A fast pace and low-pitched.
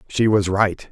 No: average, 195 wpm; low, 100 Hz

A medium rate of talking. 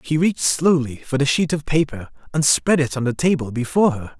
No: fast, 230 wpm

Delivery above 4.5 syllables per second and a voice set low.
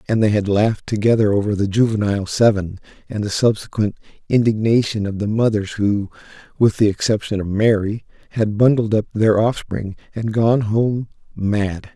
Yes: 5.1 syllables/s; low, 105 Hz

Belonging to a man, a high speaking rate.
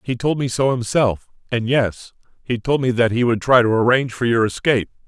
Yes: male; fast, 215 wpm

